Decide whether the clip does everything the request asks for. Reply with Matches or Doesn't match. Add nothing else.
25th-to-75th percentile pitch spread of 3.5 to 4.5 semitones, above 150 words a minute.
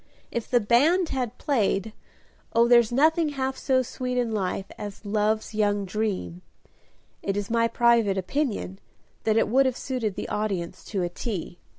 Matches